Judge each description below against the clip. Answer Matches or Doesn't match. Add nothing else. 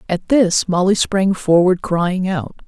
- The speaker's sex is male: Doesn't match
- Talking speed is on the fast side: Doesn't match